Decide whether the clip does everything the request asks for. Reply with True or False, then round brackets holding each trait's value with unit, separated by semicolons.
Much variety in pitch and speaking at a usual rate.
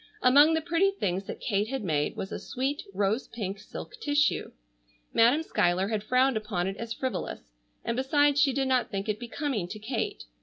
True (5.7 semitones; 190 wpm)